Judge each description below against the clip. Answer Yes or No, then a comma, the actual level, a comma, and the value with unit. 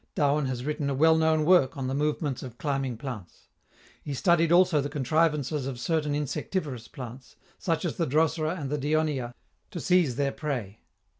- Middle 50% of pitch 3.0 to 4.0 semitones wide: Yes, average, 3.3 semitones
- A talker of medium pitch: Yes, medium, 145 Hz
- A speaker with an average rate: Yes, average, 175 wpm